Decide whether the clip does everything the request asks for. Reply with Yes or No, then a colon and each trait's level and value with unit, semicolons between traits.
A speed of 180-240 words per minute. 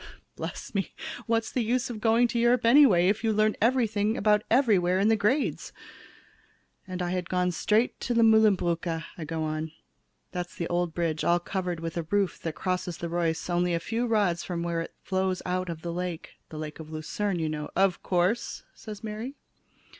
Yes: average, 190 wpm